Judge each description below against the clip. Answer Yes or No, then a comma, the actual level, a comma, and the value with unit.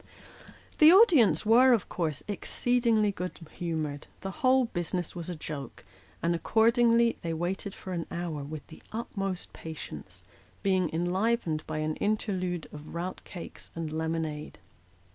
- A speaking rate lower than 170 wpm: Yes, average, 140 wpm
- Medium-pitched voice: Yes, medium, 180 Hz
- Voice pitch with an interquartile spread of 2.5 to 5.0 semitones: No, wide, 5.6 semitones